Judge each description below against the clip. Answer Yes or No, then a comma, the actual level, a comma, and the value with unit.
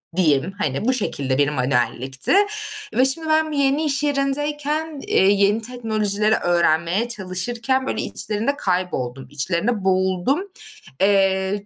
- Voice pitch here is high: Yes, high, 205 Hz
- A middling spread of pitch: No, wide, 7.3 semitones